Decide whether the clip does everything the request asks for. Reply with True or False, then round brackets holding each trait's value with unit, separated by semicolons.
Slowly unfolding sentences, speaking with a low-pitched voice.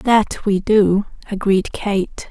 False (130 wpm; 205 Hz)